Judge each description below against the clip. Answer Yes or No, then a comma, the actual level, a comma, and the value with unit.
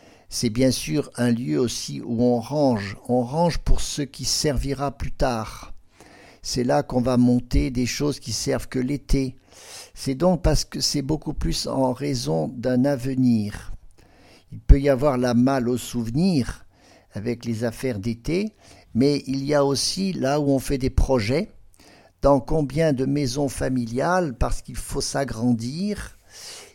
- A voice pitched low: Yes, low, 130 Hz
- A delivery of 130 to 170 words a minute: Yes, average, 160 wpm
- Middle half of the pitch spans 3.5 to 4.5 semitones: No, average, 3.0 semitones